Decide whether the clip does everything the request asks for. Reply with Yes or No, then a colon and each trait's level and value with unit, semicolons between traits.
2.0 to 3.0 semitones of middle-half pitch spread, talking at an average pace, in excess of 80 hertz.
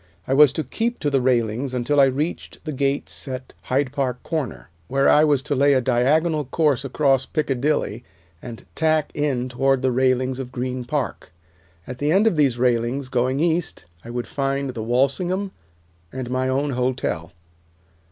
Yes: average, 2.7 semitones; average, 170 wpm; low, 135 Hz